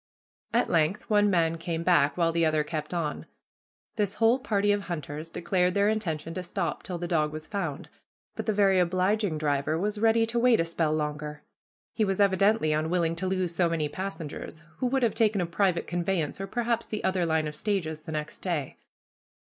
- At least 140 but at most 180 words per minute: No, average, 200 wpm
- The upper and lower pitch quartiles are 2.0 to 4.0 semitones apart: No, average, 4.4 semitones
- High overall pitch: No, medium, 175 Hz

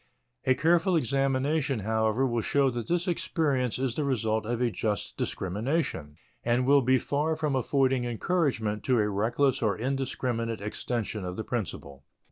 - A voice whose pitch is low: Yes, low, 125 Hz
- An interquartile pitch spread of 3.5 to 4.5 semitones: Yes, average, 4.0 semitones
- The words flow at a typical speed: Yes, average, 155 wpm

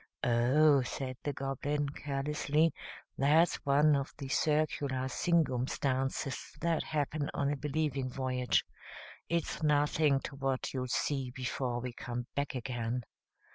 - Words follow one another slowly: Yes, slow, 125 wpm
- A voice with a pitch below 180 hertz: Yes, medium, 140 Hz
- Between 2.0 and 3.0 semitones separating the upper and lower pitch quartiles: Yes, narrow, 2.5 semitones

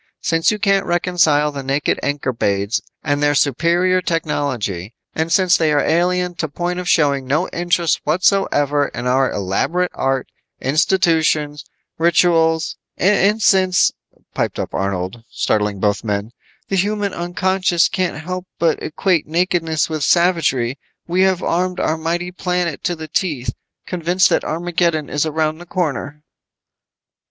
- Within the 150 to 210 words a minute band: No, average, 140 wpm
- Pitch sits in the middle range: Yes, medium, 165 Hz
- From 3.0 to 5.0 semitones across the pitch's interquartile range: Yes, average, 3.9 semitones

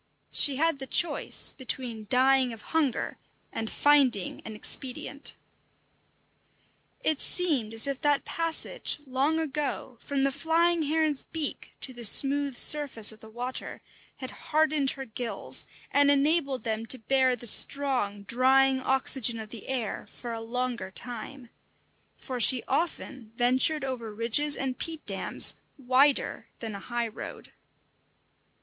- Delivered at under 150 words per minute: Yes, average, 140 wpm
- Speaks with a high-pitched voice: Yes, very high, 260 Hz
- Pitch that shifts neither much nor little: Yes, average, 3.4 semitones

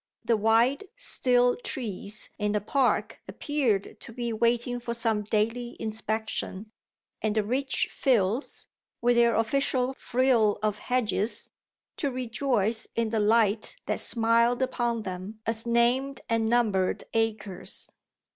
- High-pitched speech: Yes, high, 230 Hz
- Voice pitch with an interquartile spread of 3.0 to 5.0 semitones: No, narrow, 2.4 semitones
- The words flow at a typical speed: No, slow, 125 wpm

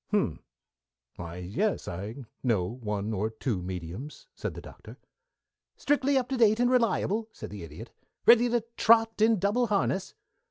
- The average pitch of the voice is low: No, high, 190 Hz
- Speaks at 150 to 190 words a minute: Yes, average, 155 wpm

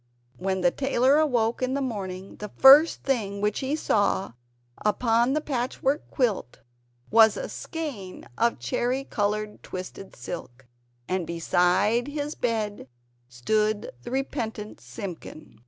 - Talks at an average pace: No, slow, 125 wpm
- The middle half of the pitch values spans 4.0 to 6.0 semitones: Yes, wide, 5.6 semitones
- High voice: Yes, high, 220 Hz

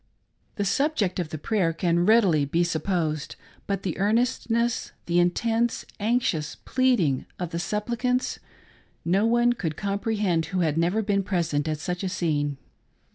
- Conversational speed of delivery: Yes, average, 155 wpm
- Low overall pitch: No, medium, 185 Hz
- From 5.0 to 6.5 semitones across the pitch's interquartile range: Yes, average, 5.3 semitones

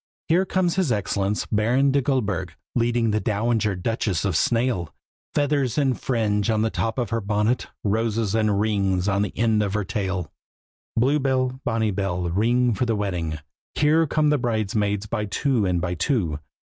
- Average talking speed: Yes, average, 175 wpm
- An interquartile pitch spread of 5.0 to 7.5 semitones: No, average, 3.9 semitones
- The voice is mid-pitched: No, low, 110 Hz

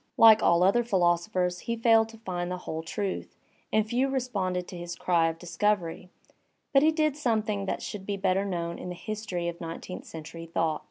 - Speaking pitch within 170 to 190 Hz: Yes, medium, 185 Hz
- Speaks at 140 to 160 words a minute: No, average, 200 wpm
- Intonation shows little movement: No, average, 4.2 semitones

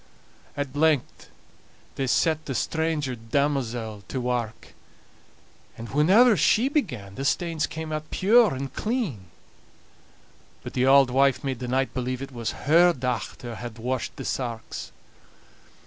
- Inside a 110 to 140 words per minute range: Yes, slow, 135 wpm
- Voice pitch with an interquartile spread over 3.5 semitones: Yes, average, 4.5 semitones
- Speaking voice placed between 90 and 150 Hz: Yes, low, 135 Hz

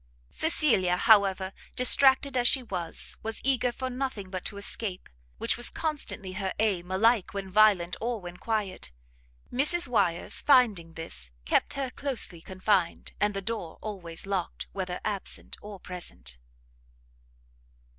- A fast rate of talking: No, slow, 135 wpm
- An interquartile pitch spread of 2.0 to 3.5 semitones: No, average, 5.0 semitones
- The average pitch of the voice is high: Yes, high, 200 Hz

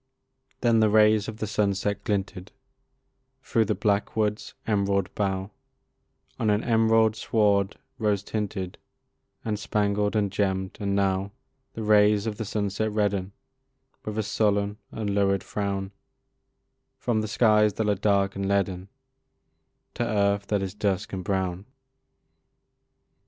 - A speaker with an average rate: No, slow, 130 wpm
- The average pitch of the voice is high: No, low, 105 Hz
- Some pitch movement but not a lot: No, narrow, 1.5 semitones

